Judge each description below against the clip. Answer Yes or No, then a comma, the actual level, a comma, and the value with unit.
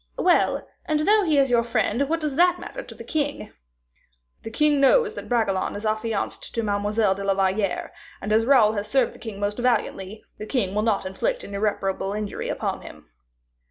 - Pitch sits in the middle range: No, high, 220 Hz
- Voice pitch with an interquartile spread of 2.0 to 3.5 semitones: No, wide, 5.4 semitones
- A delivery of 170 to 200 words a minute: Yes, average, 195 wpm